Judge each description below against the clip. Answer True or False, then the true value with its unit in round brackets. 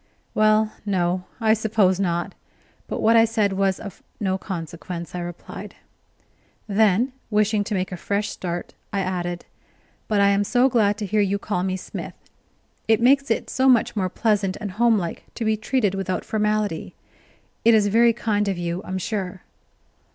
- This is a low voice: False (205 Hz)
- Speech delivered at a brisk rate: False (170 wpm)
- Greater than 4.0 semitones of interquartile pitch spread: False (2.8 semitones)